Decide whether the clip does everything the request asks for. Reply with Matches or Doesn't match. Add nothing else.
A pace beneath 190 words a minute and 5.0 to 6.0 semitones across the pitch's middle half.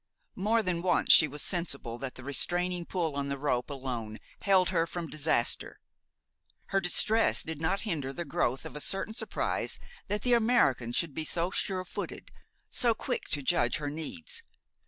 Matches